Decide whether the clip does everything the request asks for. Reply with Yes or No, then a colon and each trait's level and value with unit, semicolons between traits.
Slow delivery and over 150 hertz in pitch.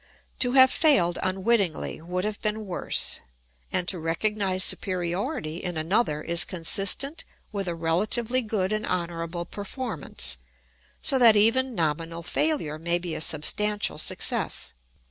Yes: slow, 130 wpm; medium, 185 Hz